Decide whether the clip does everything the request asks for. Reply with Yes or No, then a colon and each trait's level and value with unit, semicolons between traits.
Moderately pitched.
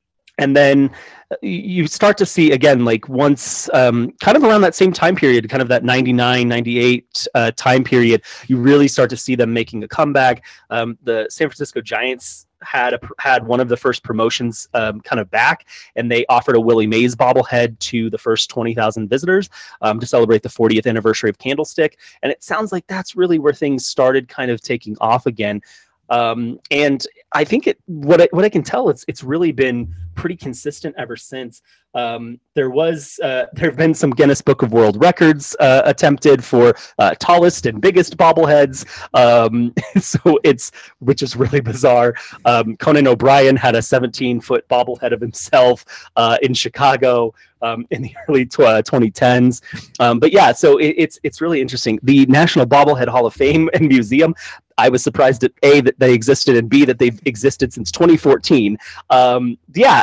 No: low, 130 Hz